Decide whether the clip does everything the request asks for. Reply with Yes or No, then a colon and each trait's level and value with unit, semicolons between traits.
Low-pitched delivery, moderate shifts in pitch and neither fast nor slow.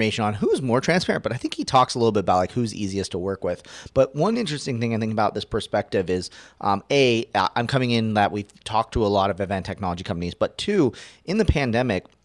No: low, 110 Hz; average, 4.5 semitones; fast, 240 wpm